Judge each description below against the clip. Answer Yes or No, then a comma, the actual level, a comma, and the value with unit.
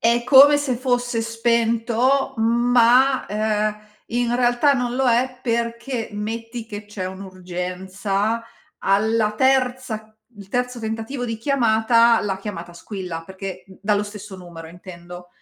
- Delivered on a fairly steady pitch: No, average, 3.6 semitones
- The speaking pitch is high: Yes, high, 225 Hz